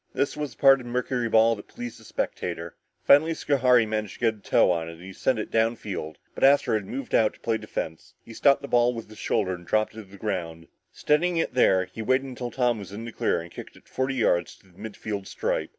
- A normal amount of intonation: Yes, average, 4.6 semitones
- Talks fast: Yes, fast, 255 wpm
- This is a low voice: Yes, low, 110 Hz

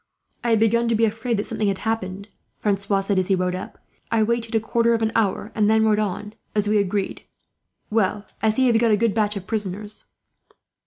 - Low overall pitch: No, high, 215 Hz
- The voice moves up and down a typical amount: No, narrow, 2.0 semitones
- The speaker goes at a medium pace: No, fast, 225 wpm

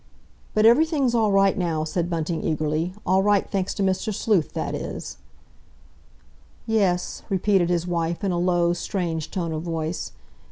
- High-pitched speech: No, medium, 180 Hz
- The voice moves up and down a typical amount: Yes, average, 3.1 semitones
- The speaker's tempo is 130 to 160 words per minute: Yes, average, 155 wpm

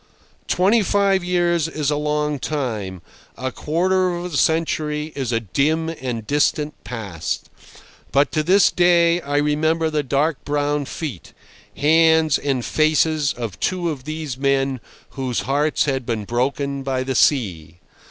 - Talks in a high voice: No, medium, 150 Hz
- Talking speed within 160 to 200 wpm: No, average, 145 wpm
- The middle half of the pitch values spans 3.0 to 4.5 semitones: Yes, average, 3.4 semitones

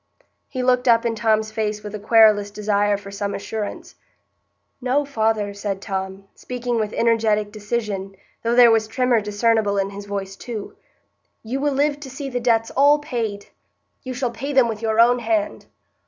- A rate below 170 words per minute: No, average, 175 wpm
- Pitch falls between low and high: No, high, 225 Hz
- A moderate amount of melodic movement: Yes, average, 3.2 semitones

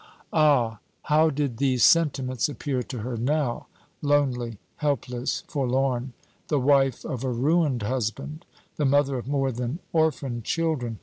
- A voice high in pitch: No, low, 135 Hz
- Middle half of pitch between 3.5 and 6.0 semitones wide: No, average, 3.1 semitones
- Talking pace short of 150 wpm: Yes, slow, 135 wpm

